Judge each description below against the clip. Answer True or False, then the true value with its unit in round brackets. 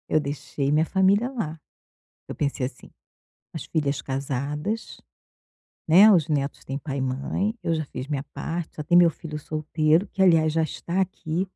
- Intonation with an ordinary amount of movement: True (3.7 semitones)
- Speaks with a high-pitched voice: False (155 Hz)